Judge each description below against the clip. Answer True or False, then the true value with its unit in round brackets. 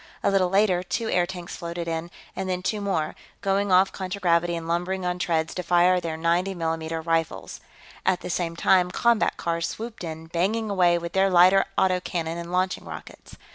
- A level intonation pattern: True (2.1 semitones)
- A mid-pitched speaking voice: True (180 Hz)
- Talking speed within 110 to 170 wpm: False (185 wpm)